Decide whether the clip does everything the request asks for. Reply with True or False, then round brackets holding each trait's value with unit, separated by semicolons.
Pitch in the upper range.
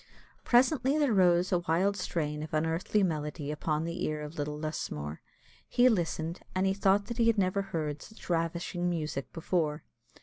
False (170 Hz)